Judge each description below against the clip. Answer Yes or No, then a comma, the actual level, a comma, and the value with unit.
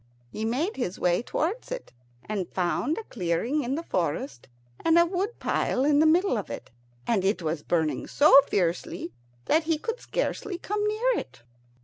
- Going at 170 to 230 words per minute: Yes, average, 175 wpm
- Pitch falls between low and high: No, very high, 270 Hz